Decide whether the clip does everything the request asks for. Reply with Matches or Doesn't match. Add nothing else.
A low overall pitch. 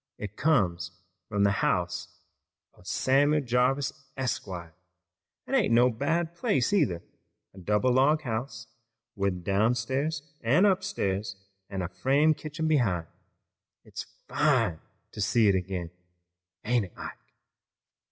Matches